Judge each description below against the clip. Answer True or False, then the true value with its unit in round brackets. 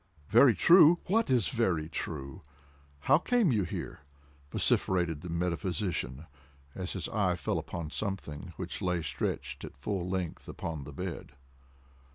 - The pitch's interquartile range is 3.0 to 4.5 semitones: False (4.9 semitones)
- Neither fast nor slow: False (130 wpm)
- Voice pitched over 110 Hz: False (90 Hz)